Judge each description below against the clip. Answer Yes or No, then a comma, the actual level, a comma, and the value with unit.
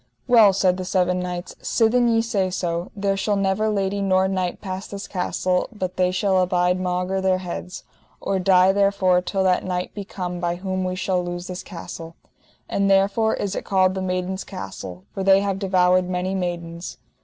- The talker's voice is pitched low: No, medium, 185 Hz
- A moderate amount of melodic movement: No, narrow, 1.4 semitones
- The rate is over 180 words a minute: Yes, average, 190 wpm